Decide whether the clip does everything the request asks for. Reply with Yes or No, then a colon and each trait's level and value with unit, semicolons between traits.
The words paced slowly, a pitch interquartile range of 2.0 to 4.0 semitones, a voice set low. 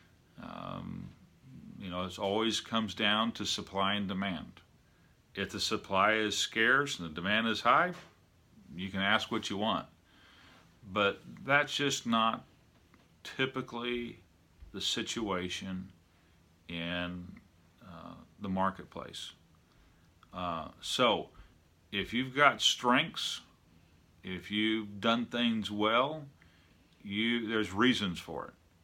No: slow, 110 wpm; average, 4.5 semitones; low, 100 Hz